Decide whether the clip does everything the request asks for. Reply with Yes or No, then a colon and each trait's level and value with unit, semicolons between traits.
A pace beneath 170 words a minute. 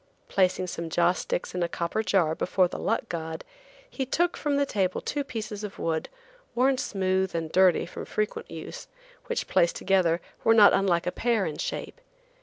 No: average, 185 wpm